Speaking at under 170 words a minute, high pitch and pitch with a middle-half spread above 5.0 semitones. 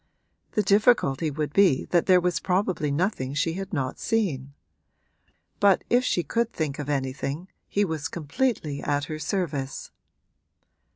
No: average, 140 wpm; medium, 160 Hz; wide, 5.5 semitones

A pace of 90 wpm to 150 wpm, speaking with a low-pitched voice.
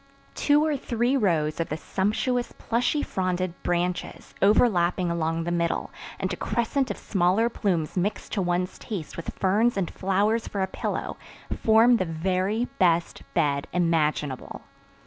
No: average, 145 wpm; medium, 185 Hz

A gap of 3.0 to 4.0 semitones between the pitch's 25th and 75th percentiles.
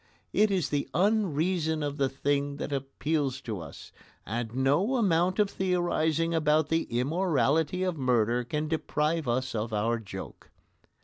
No: average, 4.4 semitones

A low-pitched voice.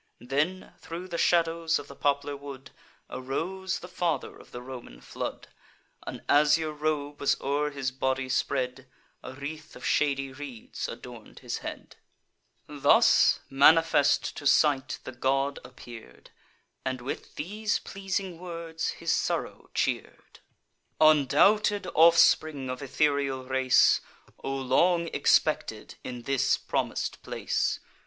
No: medium, 145 Hz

